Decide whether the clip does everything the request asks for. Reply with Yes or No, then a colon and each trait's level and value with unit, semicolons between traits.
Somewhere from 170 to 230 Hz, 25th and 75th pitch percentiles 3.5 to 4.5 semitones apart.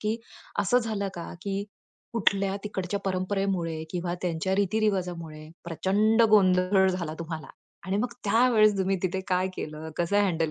No: high, 190 Hz; average, 2.8 semitones